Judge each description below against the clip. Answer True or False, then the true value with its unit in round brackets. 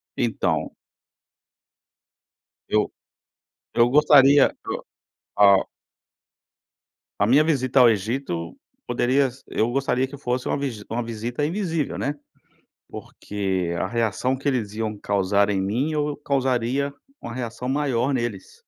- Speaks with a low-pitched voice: True (125 Hz)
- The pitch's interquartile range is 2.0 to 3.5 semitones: False (4.5 semitones)